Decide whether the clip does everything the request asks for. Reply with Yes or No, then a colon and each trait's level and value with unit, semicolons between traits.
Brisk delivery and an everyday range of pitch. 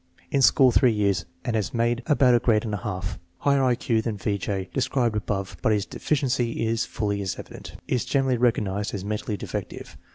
Yes: fast, 215 wpm; average, 3.4 semitones